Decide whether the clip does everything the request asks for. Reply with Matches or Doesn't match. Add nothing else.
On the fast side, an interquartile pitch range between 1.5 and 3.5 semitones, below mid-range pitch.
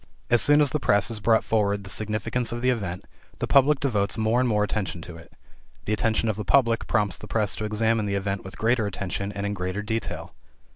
Matches